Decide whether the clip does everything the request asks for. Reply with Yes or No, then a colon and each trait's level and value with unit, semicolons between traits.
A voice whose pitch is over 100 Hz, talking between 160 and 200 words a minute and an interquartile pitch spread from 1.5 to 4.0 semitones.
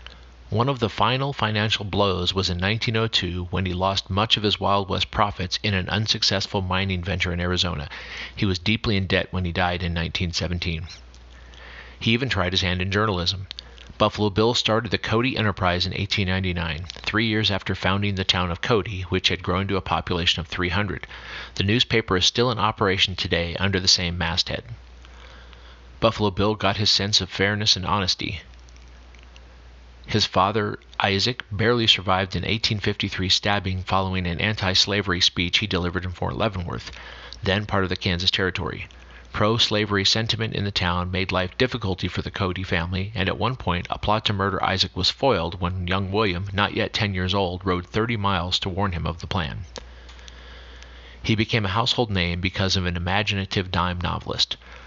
No: very low, 95 Hz; average, 175 wpm; average, 2.8 semitones